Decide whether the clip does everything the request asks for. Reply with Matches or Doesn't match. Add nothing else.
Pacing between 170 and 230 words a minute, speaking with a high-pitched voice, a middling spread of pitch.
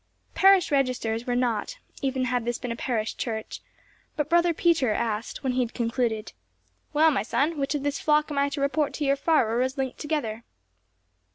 Matches